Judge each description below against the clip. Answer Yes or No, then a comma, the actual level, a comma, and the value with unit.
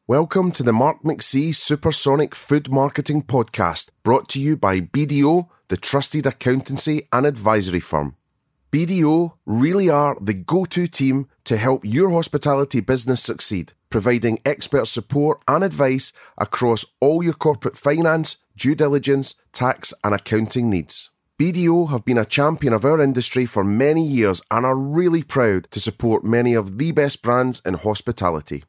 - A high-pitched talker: No, low, 135 Hz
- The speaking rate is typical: Yes, average, 155 wpm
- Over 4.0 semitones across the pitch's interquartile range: Yes, average, 4.7 semitones